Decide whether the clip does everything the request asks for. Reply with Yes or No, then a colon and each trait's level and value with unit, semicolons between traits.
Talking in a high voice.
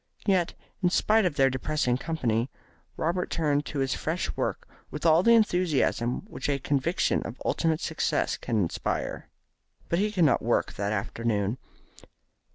No: medium, 145 Hz